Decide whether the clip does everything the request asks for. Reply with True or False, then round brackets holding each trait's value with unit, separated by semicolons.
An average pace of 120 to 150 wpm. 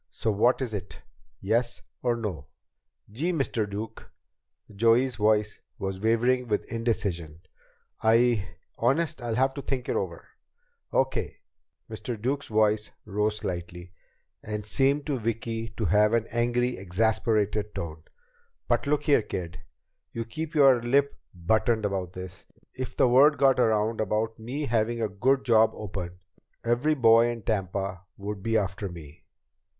True (145 wpm)